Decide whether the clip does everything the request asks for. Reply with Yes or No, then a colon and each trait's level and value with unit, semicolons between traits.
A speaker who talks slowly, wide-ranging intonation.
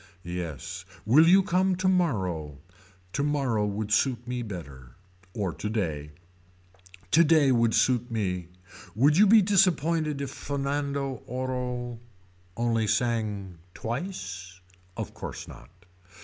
Yes: slow, 105 wpm; wide, 6.1 semitones